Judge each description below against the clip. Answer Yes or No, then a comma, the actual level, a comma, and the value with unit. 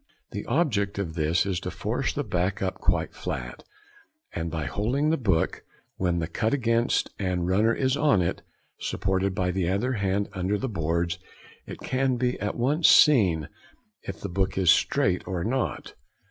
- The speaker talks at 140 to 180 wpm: Yes, average, 175 wpm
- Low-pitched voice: Yes, very low, 95 Hz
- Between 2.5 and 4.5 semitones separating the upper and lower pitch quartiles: No, average, 5.1 semitones